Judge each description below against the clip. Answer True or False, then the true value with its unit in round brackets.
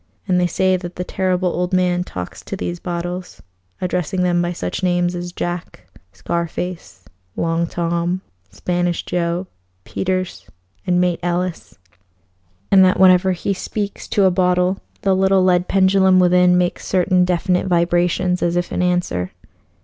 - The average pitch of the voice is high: False (180 Hz)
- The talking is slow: False (150 wpm)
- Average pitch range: False (0.9 semitones)